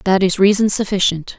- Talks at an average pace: Yes, average, 175 wpm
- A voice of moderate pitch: No, high, 195 Hz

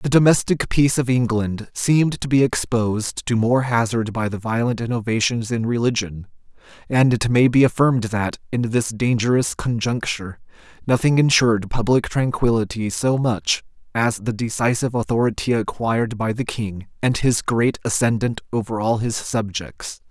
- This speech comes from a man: Yes, male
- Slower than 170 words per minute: Yes, average, 150 wpm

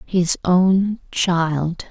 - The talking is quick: No, slow, 95 wpm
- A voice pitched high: No, medium, 180 Hz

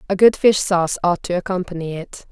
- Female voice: Yes, female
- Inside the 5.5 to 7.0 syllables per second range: Yes, 5.8 syllables/s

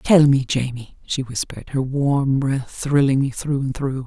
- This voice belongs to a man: No, female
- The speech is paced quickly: No, average, 190 wpm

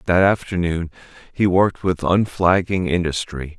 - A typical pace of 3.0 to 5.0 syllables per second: Yes, 4.7 syllables/s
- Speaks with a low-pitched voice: Yes, very low, 90 Hz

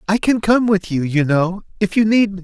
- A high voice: Yes, high, 195 Hz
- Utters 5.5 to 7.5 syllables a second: No, 5.2 syllables/s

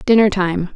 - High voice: Yes, high, 195 Hz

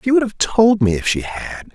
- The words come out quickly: Yes, fast, 275 wpm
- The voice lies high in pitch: No, medium, 155 Hz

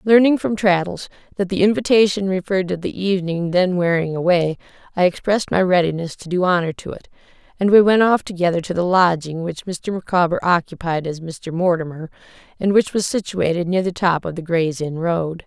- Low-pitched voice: No, medium, 180 Hz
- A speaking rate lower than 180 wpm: No, average, 190 wpm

